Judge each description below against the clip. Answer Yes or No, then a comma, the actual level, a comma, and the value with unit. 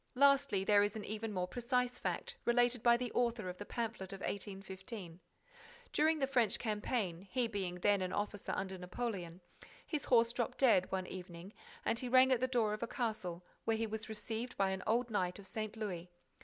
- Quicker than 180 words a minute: Yes, average, 195 wpm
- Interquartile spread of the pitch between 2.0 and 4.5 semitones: Yes, average, 4.1 semitones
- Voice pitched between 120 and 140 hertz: No, high, 215 Hz